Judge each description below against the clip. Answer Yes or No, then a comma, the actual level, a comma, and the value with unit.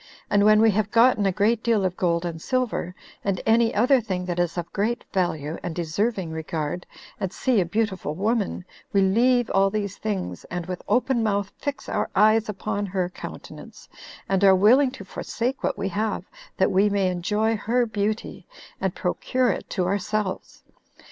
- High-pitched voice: Yes, high, 200 Hz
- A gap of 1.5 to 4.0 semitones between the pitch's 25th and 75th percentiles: Yes, average, 3.5 semitones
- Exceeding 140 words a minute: Yes, average, 180 wpm